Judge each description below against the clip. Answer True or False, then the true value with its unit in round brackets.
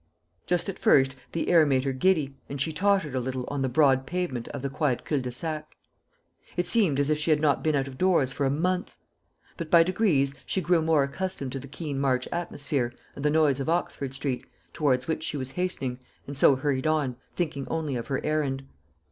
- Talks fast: True (215 wpm)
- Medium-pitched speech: True (145 Hz)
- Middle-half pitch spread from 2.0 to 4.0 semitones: True (3.4 semitones)